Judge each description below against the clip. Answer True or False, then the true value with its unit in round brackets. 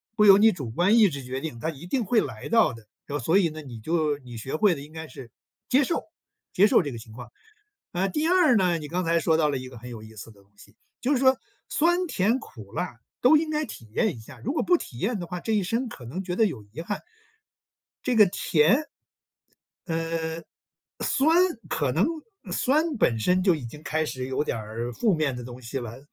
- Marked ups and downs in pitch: True (9.0 semitones)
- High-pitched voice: False (160 Hz)